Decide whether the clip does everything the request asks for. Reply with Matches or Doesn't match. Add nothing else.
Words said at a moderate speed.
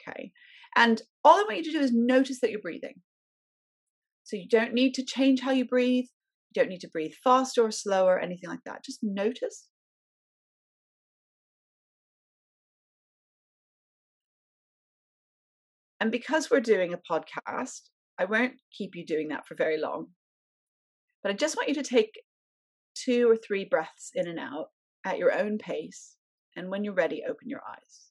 Matches